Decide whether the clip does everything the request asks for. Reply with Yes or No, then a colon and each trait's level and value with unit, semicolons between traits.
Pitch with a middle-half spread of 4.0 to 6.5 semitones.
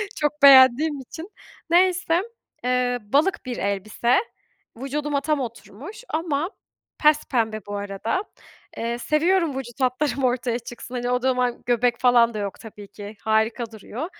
Yes: average, 4.3 semitones